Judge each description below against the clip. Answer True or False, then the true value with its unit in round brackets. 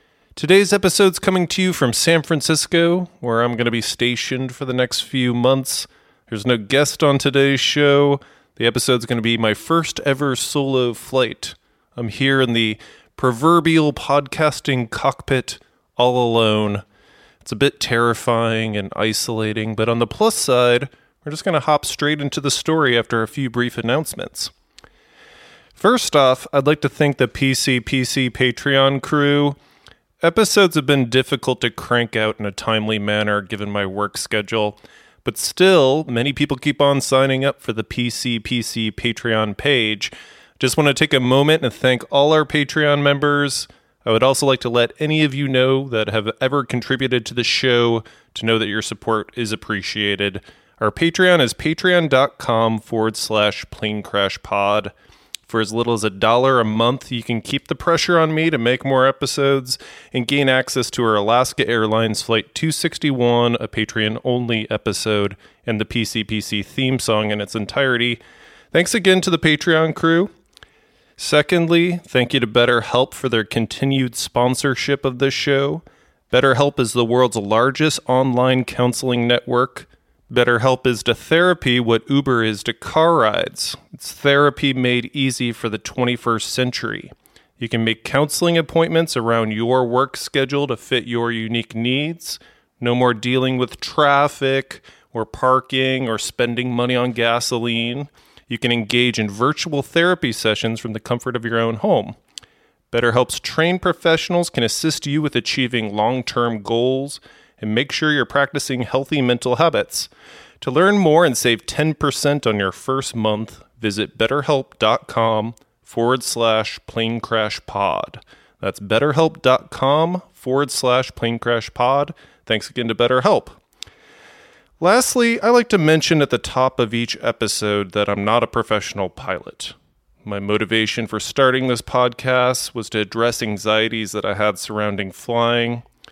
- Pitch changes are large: False (3.9 semitones)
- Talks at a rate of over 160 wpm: False (155 wpm)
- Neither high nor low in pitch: False (125 Hz)